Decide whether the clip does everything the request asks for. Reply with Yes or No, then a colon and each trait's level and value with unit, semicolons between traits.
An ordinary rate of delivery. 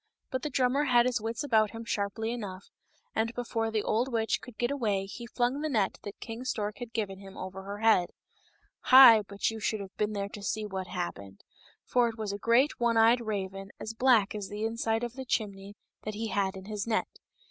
No: fast, 225 wpm